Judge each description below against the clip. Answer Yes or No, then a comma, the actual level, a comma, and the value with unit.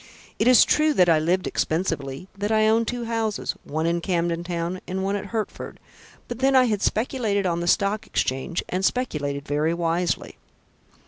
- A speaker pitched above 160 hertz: Yes, medium, 185 Hz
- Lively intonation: No, average, 4.6 semitones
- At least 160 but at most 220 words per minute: Yes, average, 180 wpm